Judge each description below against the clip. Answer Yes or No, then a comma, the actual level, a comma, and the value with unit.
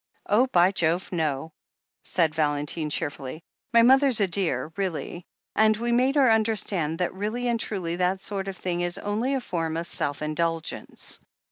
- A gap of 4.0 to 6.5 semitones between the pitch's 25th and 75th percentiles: Yes, average, 5.1 semitones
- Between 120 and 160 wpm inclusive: No, average, 170 wpm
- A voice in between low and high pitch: Yes, medium, 180 Hz